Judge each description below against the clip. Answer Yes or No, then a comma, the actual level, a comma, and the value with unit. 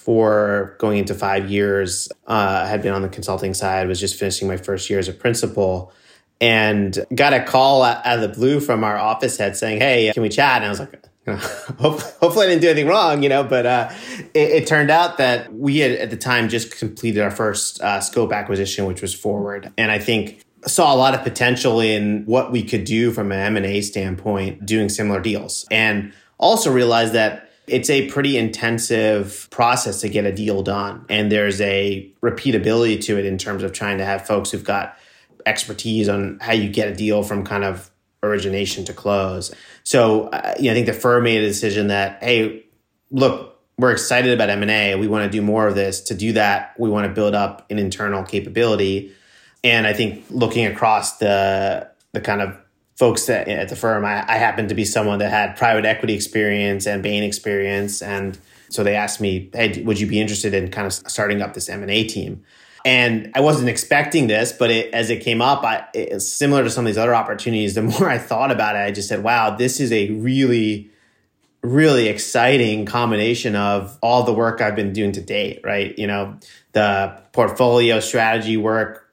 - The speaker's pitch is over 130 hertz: No, low, 105 Hz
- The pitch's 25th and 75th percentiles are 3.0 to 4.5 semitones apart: No, narrow, 2.4 semitones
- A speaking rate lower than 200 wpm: No, fast, 205 wpm